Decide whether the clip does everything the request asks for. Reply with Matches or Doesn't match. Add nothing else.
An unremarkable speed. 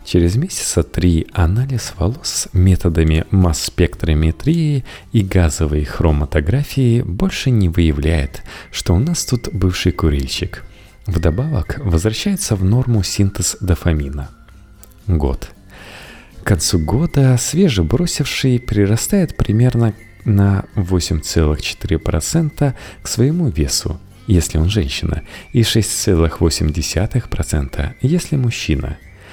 Doesn't match